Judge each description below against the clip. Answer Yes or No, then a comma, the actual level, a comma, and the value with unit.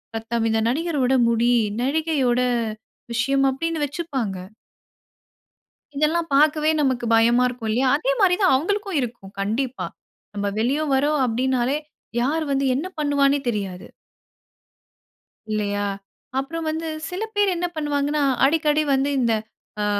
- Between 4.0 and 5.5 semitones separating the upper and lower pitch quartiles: Yes, average, 4.5 semitones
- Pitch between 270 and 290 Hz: Yes, very high, 275 Hz